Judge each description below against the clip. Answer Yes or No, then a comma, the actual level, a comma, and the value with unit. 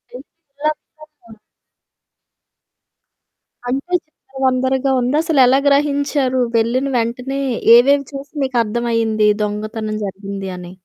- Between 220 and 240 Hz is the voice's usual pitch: No, very high, 255 Hz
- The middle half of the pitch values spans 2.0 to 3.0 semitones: No, average, 3.8 semitones